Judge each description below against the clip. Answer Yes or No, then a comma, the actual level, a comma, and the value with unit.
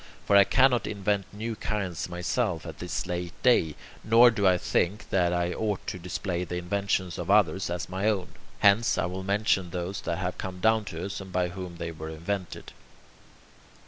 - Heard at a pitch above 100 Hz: No, very low, 95 Hz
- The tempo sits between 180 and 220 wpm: Yes, average, 190 wpm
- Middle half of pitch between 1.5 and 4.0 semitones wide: Yes, narrow, 2.6 semitones